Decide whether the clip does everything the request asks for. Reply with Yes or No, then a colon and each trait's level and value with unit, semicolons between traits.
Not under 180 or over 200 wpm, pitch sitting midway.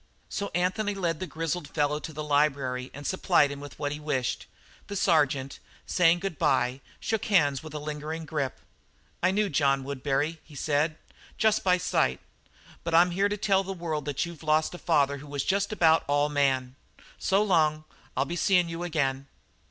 Yes: average, 185 wpm; medium, 155 Hz